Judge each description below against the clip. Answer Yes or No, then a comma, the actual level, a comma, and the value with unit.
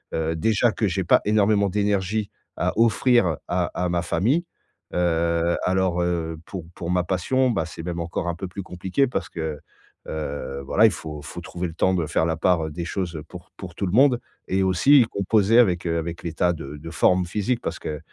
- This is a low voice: Yes, very low, 90 Hz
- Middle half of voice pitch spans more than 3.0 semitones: Yes, average, 3.4 semitones